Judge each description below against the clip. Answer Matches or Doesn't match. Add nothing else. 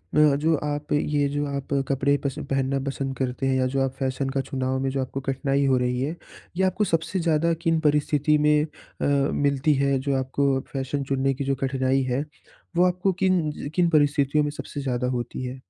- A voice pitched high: Doesn't match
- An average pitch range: Doesn't match